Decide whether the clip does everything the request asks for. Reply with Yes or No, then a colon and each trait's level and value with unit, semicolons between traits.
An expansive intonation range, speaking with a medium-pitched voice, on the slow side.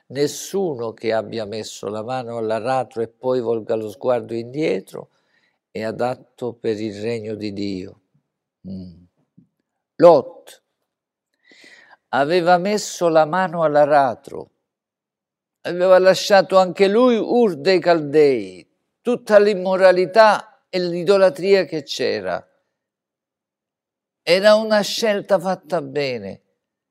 Yes: wide, 8.7 semitones; medium, 160 Hz; slow, 100 wpm